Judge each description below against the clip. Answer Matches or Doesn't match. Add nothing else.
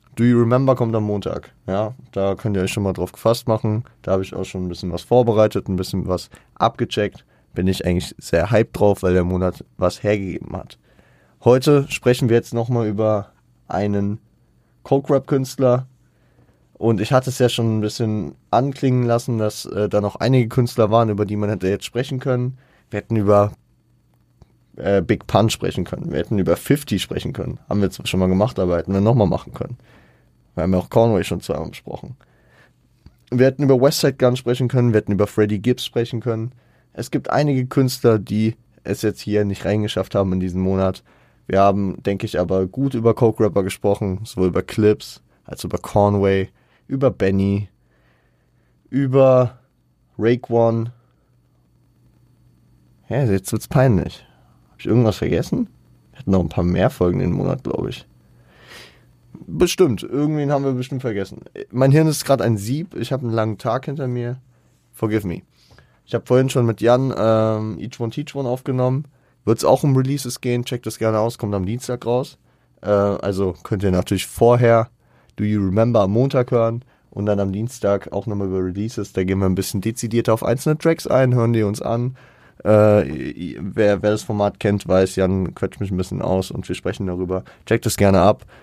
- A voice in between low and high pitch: Doesn't match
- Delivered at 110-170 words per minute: Doesn't match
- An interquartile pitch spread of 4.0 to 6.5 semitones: Matches